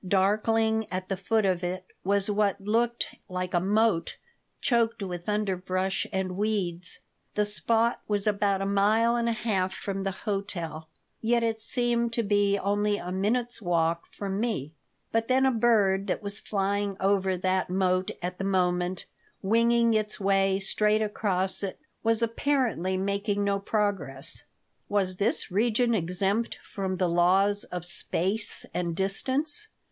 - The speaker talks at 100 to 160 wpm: Yes, average, 150 wpm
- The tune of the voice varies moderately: Yes, average, 3.0 semitones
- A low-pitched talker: No, high, 200 Hz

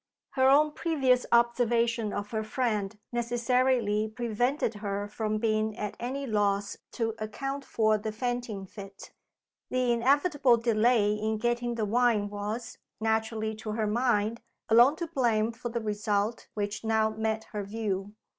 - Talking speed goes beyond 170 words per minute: No, average, 145 wpm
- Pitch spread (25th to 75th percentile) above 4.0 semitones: No, narrow, 2.4 semitones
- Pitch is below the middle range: No, high, 225 Hz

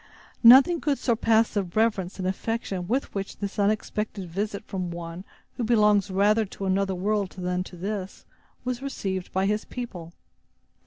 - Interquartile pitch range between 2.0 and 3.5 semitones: Yes, average, 2.9 semitones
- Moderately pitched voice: No, high, 200 Hz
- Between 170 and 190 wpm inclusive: No, average, 155 wpm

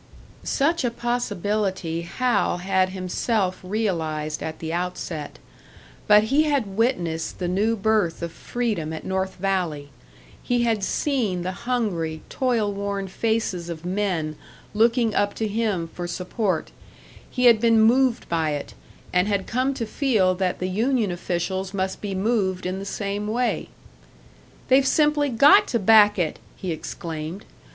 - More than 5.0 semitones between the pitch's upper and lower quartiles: No, average, 4.3 semitones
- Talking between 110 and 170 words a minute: Yes, average, 145 wpm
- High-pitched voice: Yes, high, 200 Hz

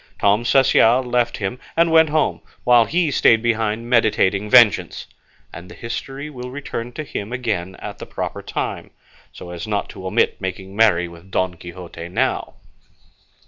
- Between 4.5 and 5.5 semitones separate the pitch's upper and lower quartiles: Yes, average, 4.9 semitones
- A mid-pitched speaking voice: No, low, 115 Hz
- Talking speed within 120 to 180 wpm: Yes, average, 160 wpm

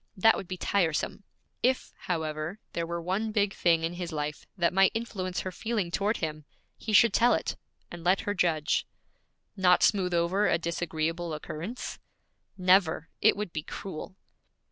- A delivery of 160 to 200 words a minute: Yes, average, 165 wpm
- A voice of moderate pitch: Yes, medium, 180 Hz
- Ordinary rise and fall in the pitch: Yes, average, 3.3 semitones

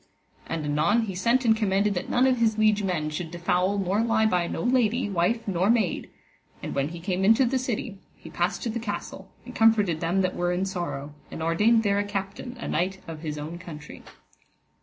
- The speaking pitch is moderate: No, high, 195 Hz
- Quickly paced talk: Yes, fast, 210 wpm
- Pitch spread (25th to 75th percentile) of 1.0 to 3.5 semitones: No, average, 4.4 semitones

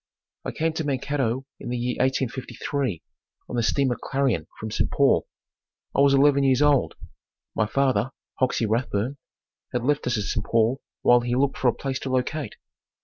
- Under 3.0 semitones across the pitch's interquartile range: Yes, narrow, 2.6 semitones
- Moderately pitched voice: No, low, 130 Hz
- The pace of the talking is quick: No, average, 175 wpm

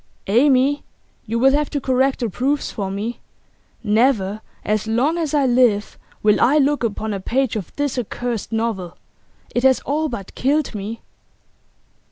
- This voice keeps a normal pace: Yes, average, 160 wpm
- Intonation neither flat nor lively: Yes, average, 4.3 semitones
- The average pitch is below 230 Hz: No, high, 240 Hz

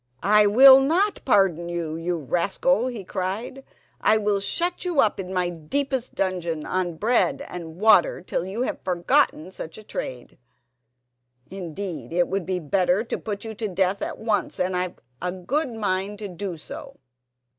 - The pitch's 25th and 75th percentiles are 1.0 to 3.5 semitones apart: No, average, 3.9 semitones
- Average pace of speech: Yes, average, 165 wpm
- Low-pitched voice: No, high, 190 Hz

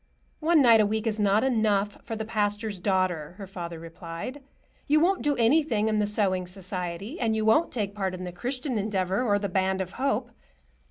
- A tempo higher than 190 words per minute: Yes, average, 200 wpm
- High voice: Yes, high, 210 Hz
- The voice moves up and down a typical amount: Yes, average, 3.6 semitones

